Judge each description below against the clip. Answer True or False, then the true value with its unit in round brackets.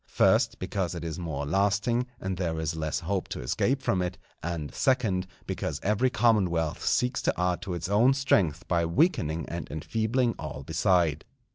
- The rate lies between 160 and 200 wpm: True (170 wpm)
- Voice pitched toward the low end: True (90 Hz)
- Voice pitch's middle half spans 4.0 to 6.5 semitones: True (5.2 semitones)